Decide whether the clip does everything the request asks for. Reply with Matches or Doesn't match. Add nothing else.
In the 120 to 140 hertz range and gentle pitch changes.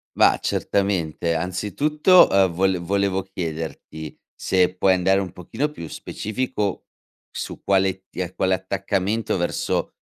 Doesn't match